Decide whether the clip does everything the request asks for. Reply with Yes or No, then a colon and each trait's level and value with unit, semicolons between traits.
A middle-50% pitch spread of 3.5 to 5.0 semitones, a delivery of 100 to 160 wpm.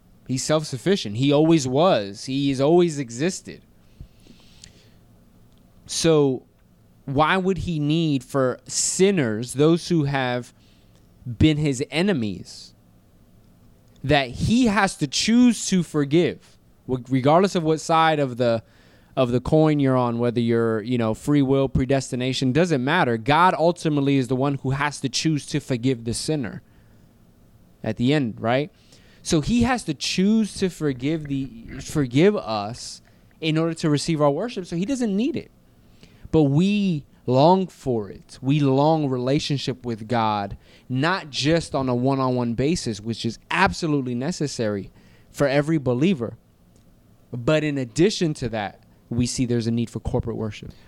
Yes: average, 4.6 semitones; average, 145 wpm